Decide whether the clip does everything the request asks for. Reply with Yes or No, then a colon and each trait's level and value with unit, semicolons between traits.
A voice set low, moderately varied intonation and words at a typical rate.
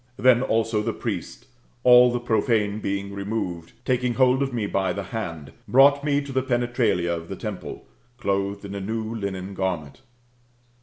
Yes: low, 110 Hz; average, 3.9 semitones; average, 165 wpm